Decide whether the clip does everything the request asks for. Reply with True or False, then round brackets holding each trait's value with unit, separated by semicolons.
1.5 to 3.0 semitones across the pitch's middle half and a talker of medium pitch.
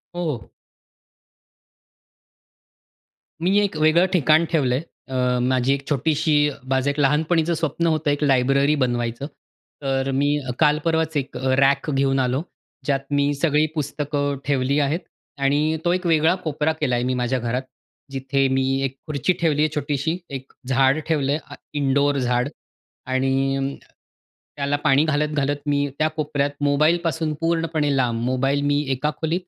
True (2.5 semitones; 145 Hz)